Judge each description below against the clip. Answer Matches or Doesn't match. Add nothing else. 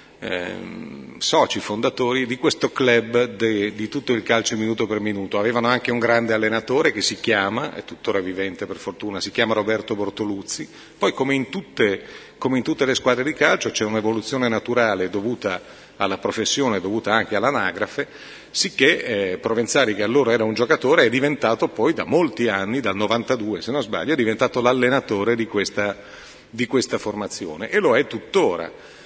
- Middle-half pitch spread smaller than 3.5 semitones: Matches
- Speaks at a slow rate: Doesn't match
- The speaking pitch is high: Doesn't match